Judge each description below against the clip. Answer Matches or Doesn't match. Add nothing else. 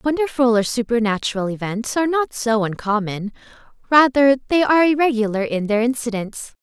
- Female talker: Matches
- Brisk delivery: Doesn't match